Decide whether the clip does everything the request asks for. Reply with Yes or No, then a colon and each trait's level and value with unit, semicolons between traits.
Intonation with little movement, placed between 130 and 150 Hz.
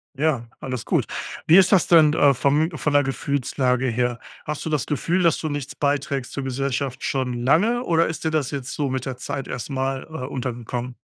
No: average, 3.1 semitones; medium, 140 Hz